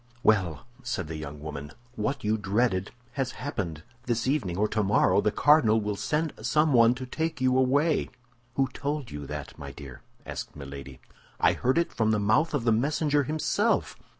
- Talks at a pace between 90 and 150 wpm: No, average, 175 wpm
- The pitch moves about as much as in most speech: No, wide, 7.1 semitones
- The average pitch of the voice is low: Yes, low, 115 Hz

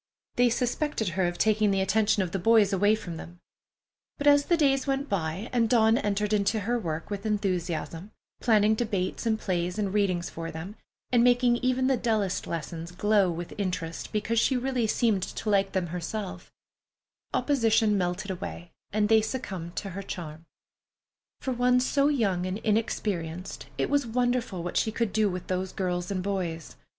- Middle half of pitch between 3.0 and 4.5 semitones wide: Yes, average, 4.2 semitones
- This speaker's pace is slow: No, average, 175 wpm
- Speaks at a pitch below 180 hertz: No, high, 205 Hz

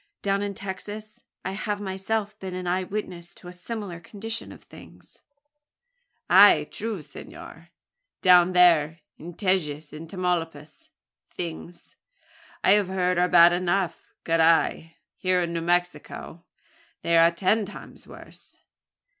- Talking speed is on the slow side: Yes, slow, 130 wpm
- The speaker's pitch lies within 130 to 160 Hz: No, medium, 180 Hz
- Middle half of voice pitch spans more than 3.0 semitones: No, average, 2.7 semitones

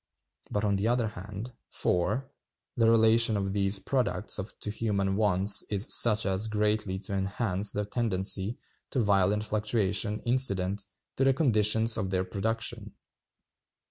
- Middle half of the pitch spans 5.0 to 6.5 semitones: No, narrow, 2.6 semitones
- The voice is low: Yes, low, 105 Hz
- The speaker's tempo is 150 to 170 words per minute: No, average, 140 wpm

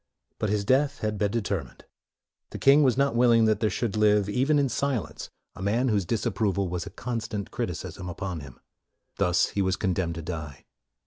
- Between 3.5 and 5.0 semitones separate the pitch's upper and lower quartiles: Yes, average, 4.2 semitones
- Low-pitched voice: Yes, low, 105 Hz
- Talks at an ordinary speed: Yes, average, 185 wpm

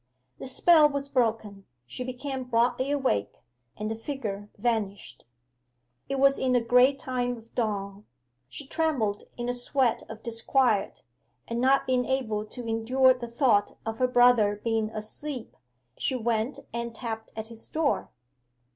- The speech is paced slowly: No, average, 150 wpm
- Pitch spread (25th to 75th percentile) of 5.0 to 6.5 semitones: No, average, 3.0 semitones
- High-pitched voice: Yes, high, 240 Hz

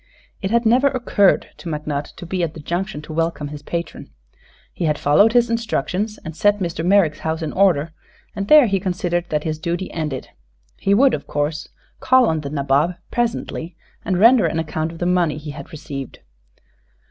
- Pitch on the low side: No, medium, 170 Hz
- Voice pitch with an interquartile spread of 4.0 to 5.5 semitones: Yes, average, 4.7 semitones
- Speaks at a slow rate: No, average, 190 wpm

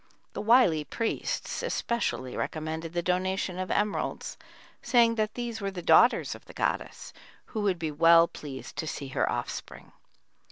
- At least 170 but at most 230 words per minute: No, average, 155 wpm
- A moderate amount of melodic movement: No, wide, 5.7 semitones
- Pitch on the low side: No, medium, 185 Hz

